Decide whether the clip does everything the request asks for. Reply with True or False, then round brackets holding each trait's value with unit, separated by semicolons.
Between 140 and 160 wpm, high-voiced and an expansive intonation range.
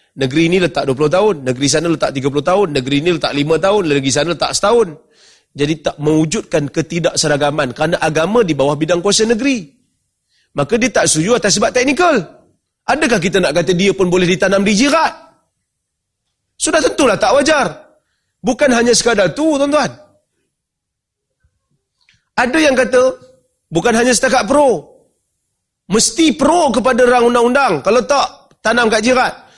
True (150 wpm; 200 Hz; 8.3 semitones)